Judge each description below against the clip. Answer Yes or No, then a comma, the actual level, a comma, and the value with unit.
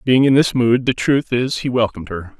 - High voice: No, low, 120 Hz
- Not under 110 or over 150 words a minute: No, fast, 250 wpm